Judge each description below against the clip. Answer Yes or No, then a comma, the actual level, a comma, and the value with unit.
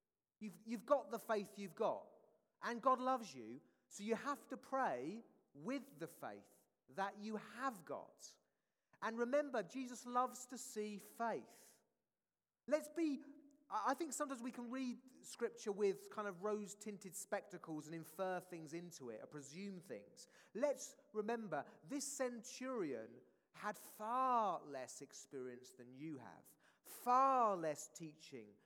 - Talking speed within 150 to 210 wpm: No, average, 140 wpm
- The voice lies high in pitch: Yes, high, 220 Hz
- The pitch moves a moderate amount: No, wide, 6.4 semitones